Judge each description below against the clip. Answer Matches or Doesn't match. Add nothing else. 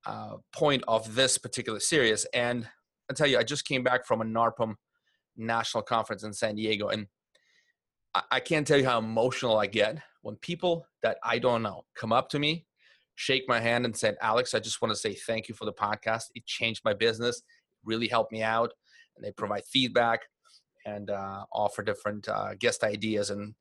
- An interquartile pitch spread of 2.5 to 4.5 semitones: Matches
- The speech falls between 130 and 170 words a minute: Doesn't match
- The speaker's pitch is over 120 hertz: Doesn't match